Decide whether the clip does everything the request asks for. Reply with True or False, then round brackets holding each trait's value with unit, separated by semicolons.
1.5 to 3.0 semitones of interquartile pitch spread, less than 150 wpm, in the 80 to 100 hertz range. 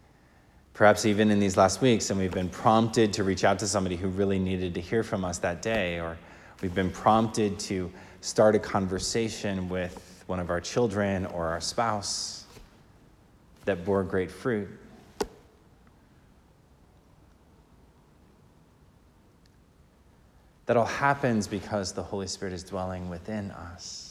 True (2.7 semitones; 135 wpm; 95 Hz)